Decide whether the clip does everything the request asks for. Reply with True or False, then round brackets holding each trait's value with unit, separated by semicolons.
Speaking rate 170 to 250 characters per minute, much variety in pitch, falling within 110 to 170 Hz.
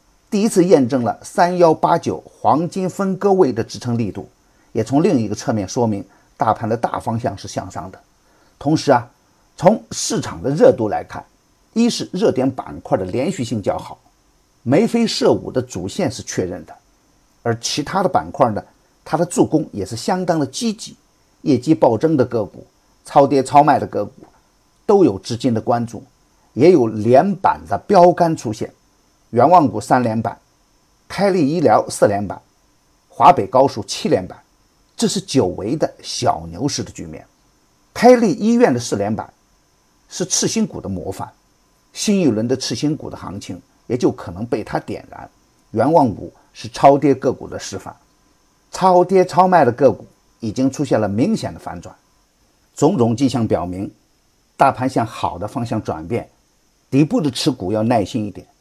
True (245 characters per minute; 7.7 semitones; 140 Hz)